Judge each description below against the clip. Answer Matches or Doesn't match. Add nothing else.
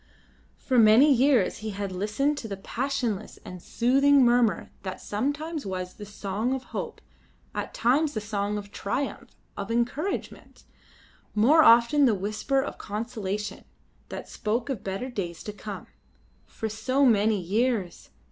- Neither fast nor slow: Matches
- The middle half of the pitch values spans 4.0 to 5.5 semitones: Matches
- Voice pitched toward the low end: Doesn't match